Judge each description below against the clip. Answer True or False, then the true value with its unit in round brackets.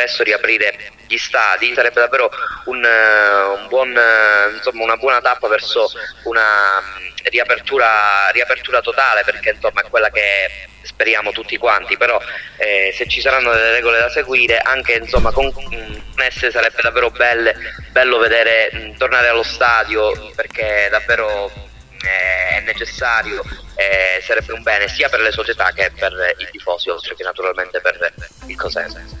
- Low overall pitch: True (115 Hz)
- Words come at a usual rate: True (145 wpm)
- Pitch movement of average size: True (4.1 semitones)